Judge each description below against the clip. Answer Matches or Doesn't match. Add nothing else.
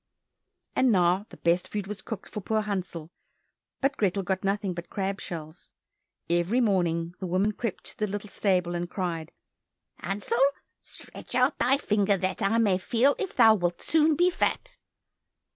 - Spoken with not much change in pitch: Doesn't match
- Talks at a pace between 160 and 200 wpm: Matches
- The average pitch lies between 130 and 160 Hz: Doesn't match